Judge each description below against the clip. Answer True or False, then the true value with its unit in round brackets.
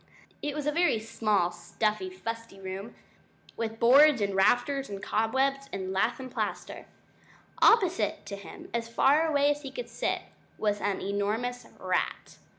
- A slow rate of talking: False (155 wpm)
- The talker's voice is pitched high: True (230 Hz)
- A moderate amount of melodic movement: False (5.7 semitones)